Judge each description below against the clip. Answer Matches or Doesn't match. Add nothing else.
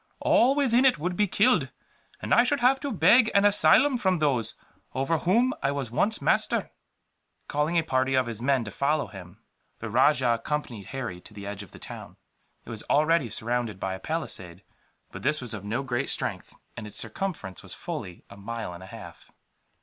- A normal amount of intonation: Doesn't match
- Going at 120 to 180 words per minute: Doesn't match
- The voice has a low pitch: Matches